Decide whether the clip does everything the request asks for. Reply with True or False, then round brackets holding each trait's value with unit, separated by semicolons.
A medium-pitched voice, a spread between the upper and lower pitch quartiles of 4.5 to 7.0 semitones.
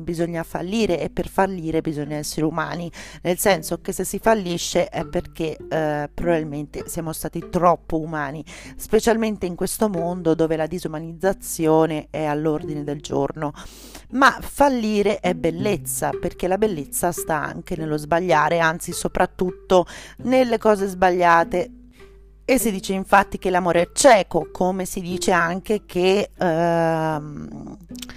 False (170 Hz; 3.3 semitones)